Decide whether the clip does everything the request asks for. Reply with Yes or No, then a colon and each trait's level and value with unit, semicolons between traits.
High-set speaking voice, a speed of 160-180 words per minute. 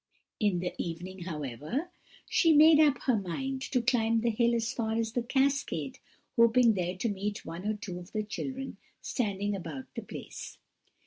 Yes: high, 220 Hz; average, 175 wpm